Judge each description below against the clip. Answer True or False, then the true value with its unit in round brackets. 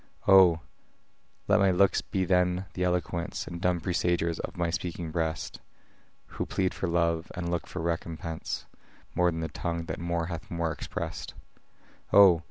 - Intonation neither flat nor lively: False (1.4 semitones)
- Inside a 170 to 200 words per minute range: False (160 wpm)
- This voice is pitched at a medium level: False (85 Hz)